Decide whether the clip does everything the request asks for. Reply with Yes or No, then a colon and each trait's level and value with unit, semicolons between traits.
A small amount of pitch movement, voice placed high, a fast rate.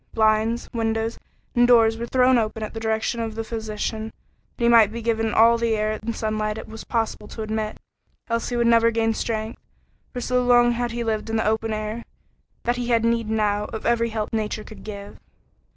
Yes: narrow, 1.3 semitones; high, 225 Hz; fast, 225 wpm